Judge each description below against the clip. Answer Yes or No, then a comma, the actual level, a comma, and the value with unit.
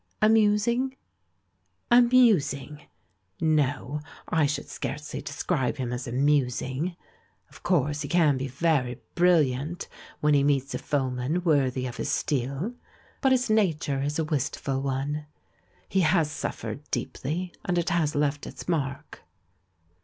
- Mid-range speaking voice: Yes, medium, 150 Hz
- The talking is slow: Yes, slow, 130 wpm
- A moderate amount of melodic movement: Yes, average, 4.3 semitones